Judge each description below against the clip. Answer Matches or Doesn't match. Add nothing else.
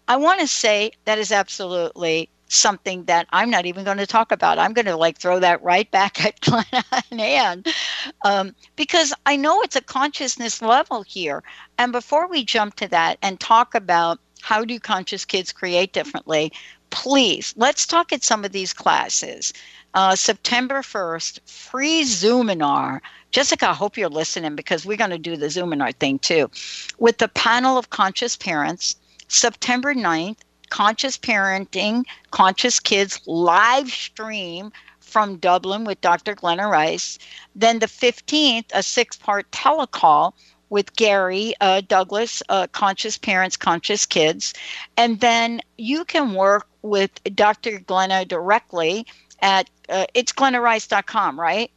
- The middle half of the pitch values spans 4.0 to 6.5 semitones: Matches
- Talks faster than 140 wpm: Matches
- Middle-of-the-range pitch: Doesn't match